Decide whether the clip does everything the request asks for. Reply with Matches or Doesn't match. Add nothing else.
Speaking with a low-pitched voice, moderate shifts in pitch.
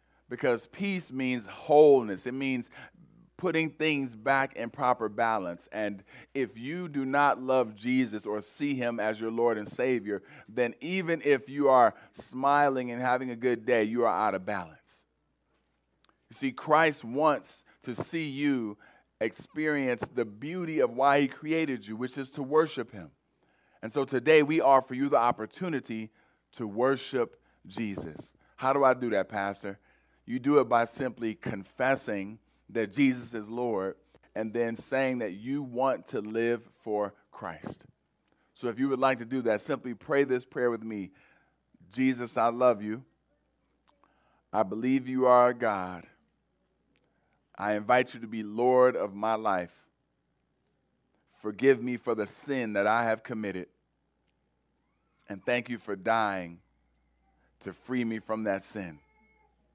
Matches